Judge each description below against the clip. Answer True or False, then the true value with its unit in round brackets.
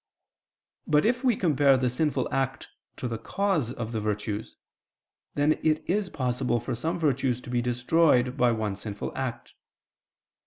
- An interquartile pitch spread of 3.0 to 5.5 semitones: True (4.5 semitones)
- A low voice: True (130 Hz)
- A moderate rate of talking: True (155 wpm)